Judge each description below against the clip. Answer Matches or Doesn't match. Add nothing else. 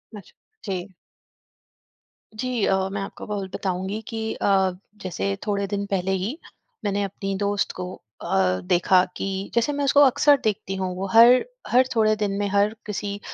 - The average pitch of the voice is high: Matches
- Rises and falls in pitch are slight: Matches